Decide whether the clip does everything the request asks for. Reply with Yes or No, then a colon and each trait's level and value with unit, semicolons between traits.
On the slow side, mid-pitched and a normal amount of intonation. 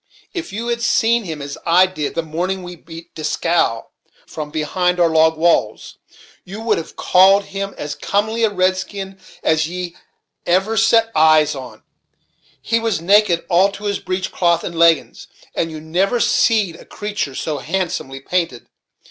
No: average, 165 wpm; medium, 180 Hz; average, 4.0 semitones